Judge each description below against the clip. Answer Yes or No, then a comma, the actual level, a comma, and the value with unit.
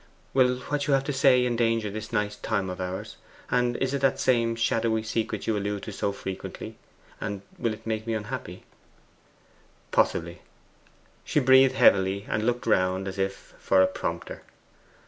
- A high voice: No, low, 110 Hz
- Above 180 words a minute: No, average, 165 wpm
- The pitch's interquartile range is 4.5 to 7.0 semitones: No, average, 3.9 semitones